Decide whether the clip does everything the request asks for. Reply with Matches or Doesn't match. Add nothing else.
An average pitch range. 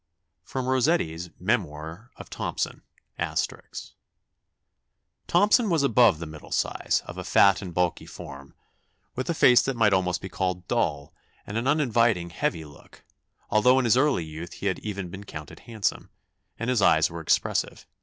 Doesn't match